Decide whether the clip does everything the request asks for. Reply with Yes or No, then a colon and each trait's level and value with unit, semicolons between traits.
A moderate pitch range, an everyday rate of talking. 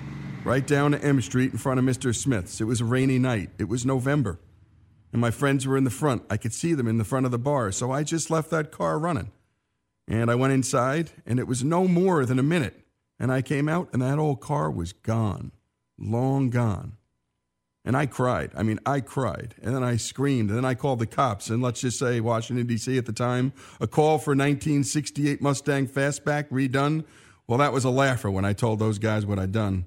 No: average, 4.0 semitones; fast, 225 wpm